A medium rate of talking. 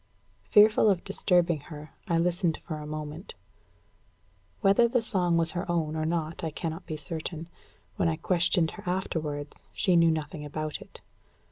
Yes: average, 160 wpm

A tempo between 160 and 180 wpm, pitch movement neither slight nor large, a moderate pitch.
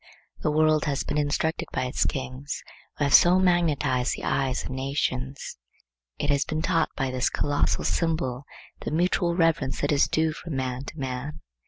Yes: average, 175 wpm; average, 3.2 semitones; medium, 145 Hz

